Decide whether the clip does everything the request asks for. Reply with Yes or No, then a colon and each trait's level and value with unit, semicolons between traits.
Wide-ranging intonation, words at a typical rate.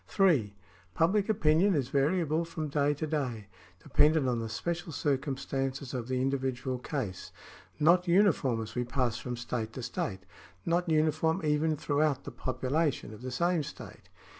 No: average, 4.3 semitones; average, 165 wpm